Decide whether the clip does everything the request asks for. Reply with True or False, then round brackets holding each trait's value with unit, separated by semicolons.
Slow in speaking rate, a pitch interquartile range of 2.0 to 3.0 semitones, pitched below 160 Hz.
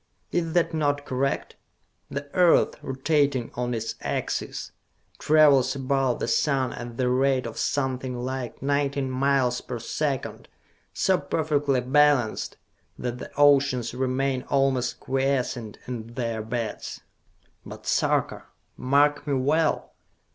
True (120 wpm; 2.4 semitones; 135 Hz)